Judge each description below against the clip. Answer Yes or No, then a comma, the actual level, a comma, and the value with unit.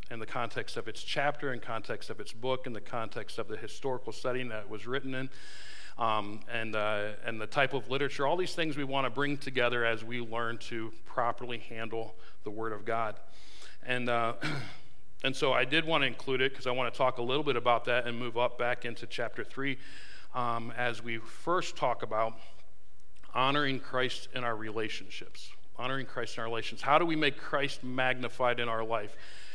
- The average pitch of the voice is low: Yes, low, 120 Hz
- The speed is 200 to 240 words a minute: Yes, fast, 205 wpm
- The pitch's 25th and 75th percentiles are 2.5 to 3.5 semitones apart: Yes, average, 2.8 semitones